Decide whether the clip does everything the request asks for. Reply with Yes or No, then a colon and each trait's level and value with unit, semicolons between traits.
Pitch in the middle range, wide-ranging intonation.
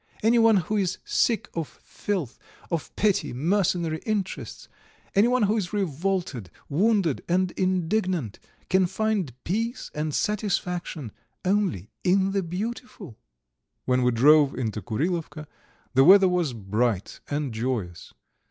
Yes: medium, 180 Hz; wide, 6.6 semitones